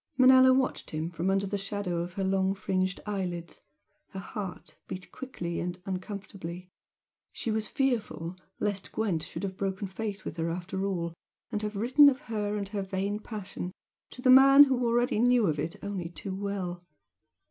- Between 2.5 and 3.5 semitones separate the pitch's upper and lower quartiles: Yes, average, 3.2 semitones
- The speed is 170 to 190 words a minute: Yes, average, 175 wpm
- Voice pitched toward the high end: Yes, high, 195 Hz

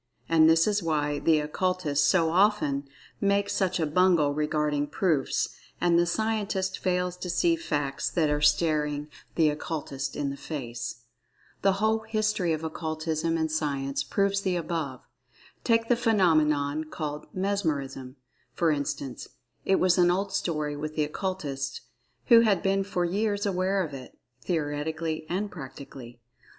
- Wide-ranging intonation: No, average, 4.4 semitones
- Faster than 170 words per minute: No, average, 145 wpm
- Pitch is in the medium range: Yes, medium, 160 Hz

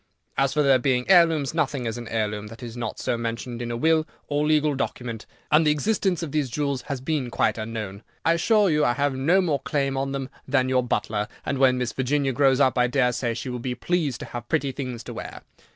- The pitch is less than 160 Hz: Yes, low, 135 Hz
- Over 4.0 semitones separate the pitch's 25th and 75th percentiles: No, average, 3.7 semitones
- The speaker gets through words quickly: Yes, fast, 235 wpm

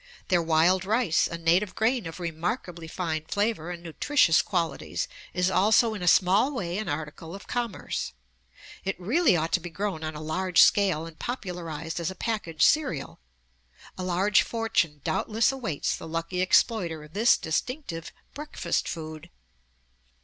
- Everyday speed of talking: Yes, average, 155 wpm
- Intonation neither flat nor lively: Yes, average, 4.4 semitones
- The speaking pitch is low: No, medium, 180 Hz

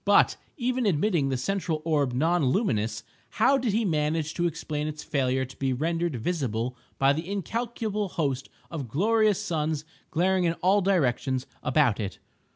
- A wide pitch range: Yes, wide, 6.0 semitones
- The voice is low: No, medium, 160 Hz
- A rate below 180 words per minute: Yes, average, 160 wpm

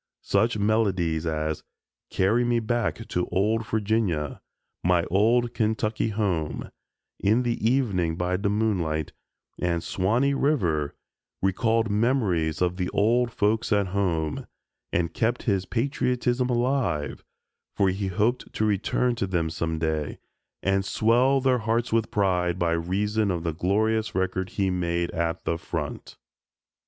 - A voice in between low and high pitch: No, low, 100 Hz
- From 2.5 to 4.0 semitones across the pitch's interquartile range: No, average, 4.6 semitones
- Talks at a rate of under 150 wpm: Yes, slow, 135 wpm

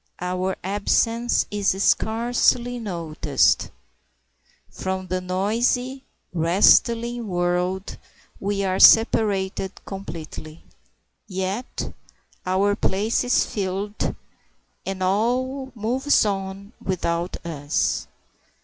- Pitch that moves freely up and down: No, average, 3.8 semitones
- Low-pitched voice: No, high, 195 Hz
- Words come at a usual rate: No, slow, 80 wpm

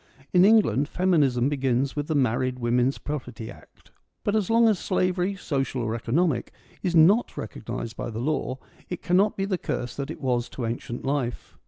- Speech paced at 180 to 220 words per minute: Yes, average, 185 wpm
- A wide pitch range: Yes, wide, 6.7 semitones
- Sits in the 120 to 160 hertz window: Yes, medium, 140 Hz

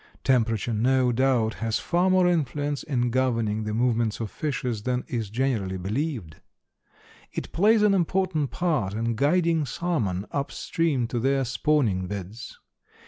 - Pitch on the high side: No, low, 125 Hz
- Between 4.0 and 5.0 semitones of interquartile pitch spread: No, wide, 5.5 semitones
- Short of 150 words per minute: Yes, average, 140 wpm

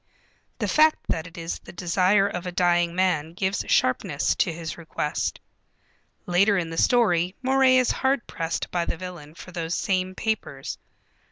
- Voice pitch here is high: No, medium, 180 Hz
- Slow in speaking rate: No, average, 165 wpm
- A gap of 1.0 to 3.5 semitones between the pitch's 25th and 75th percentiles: Yes, average, 3.1 semitones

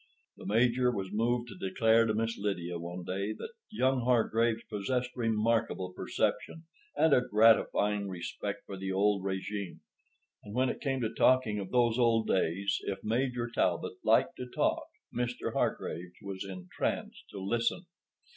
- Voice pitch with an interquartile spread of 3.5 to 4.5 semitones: Yes, average, 3.8 semitones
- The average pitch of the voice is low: Yes, low, 110 Hz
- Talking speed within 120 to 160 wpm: Yes, average, 150 wpm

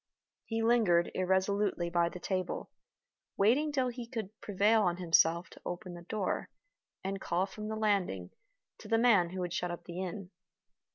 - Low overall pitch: No, high, 190 Hz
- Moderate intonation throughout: Yes, average, 3.8 semitones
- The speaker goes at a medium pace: Yes, average, 170 wpm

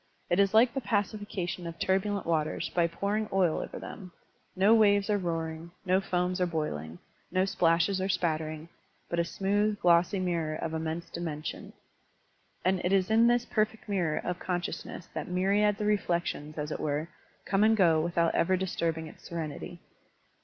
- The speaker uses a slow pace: No, average, 175 wpm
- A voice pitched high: No, medium, 180 Hz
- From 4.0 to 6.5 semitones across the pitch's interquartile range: No, average, 3.3 semitones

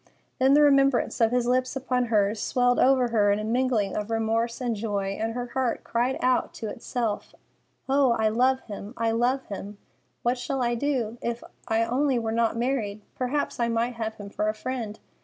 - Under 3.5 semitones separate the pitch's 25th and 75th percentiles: Yes, narrow, 2.5 semitones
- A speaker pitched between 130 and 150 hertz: No, high, 235 Hz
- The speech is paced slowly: No, average, 195 wpm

